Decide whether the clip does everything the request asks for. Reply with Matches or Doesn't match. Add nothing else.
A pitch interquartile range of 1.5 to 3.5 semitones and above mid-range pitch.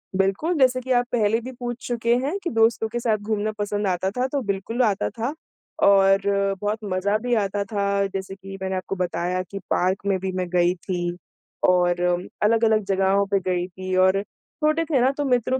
Doesn't match